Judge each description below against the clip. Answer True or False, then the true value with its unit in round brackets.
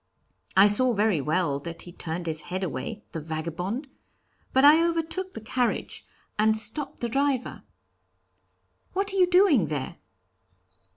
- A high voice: True (220 Hz)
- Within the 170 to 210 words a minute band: False (140 wpm)